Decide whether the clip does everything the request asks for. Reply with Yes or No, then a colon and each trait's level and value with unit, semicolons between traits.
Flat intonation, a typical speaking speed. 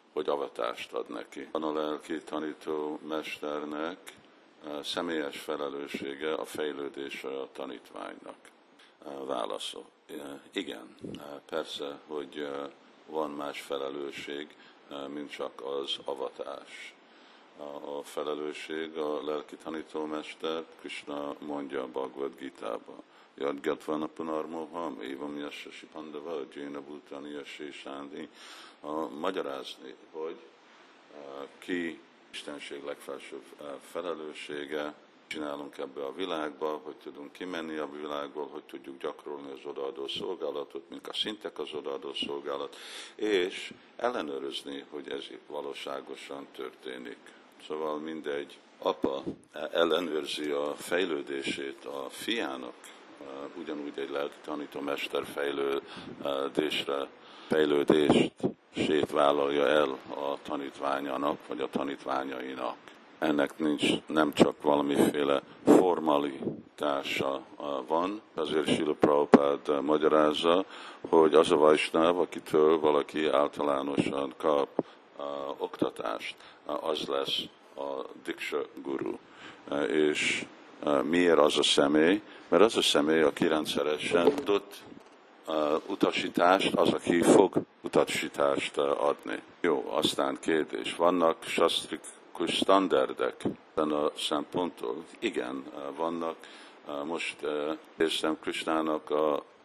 No: narrow, 1.9 semitones; slow, 95 wpm